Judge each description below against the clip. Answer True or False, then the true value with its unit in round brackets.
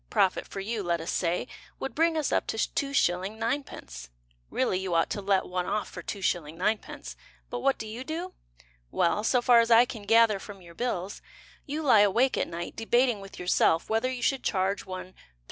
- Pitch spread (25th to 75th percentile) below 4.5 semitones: False (5.0 semitones)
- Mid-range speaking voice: False (210 Hz)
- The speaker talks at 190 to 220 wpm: True (200 wpm)